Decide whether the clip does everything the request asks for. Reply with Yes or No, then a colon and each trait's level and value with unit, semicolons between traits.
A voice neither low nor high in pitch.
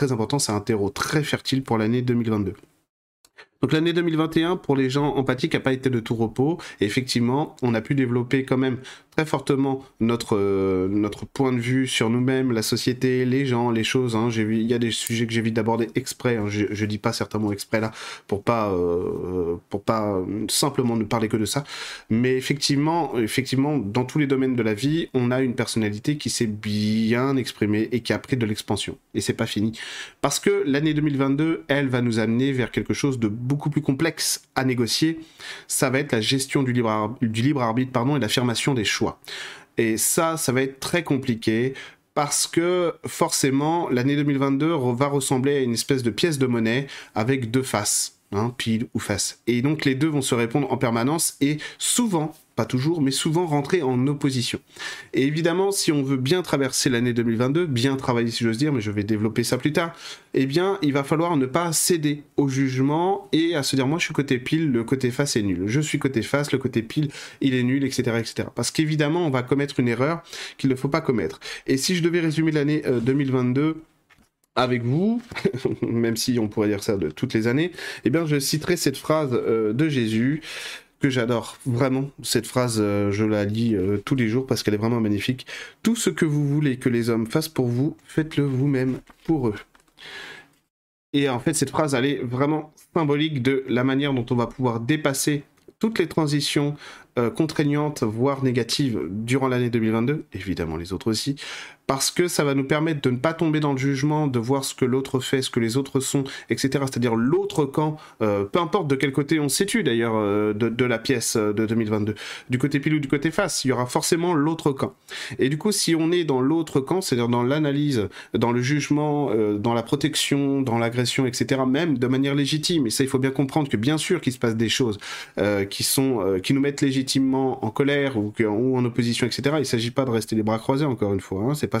No: low, 130 Hz